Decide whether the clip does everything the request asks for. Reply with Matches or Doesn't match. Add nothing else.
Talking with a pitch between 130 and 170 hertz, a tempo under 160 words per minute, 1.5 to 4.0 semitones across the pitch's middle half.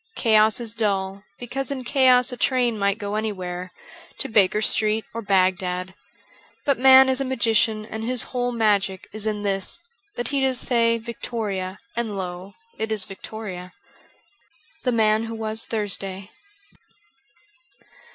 Doesn't match